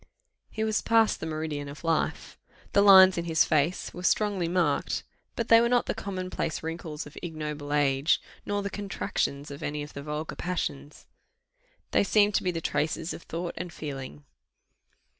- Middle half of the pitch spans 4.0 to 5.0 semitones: Yes, average, 4.7 semitones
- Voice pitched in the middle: Yes, medium, 165 Hz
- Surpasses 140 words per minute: Yes, average, 180 wpm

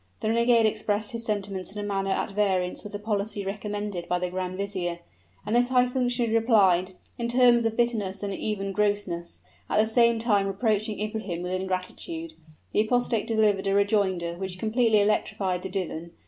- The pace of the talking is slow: No, average, 175 wpm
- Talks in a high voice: Yes, high, 205 Hz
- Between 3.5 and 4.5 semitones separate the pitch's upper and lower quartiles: No, average, 2.9 semitones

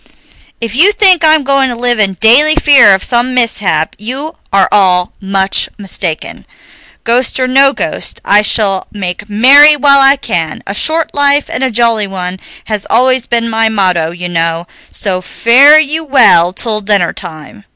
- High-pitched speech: Yes, high, 225 Hz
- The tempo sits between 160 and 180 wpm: Yes, average, 165 wpm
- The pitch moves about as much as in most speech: No, wide, 6.0 semitones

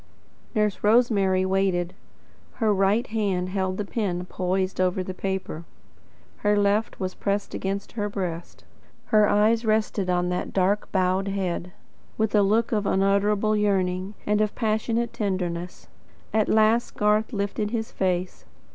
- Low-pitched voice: No, high, 200 Hz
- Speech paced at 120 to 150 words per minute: Yes, average, 140 wpm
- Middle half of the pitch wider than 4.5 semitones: No, narrow, 2.4 semitones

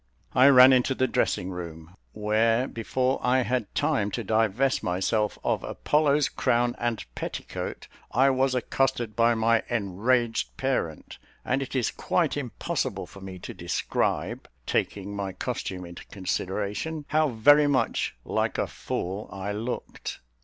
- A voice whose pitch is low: Yes, low, 115 Hz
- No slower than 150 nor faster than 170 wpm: No, average, 140 wpm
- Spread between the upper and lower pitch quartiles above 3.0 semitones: Yes, average, 4.6 semitones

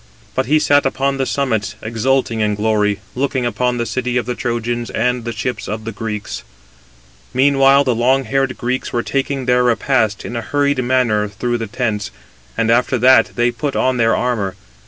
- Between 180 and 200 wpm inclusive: Yes, average, 185 wpm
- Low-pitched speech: Yes, low, 120 Hz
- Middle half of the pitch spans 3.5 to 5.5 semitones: No, average, 2.7 semitones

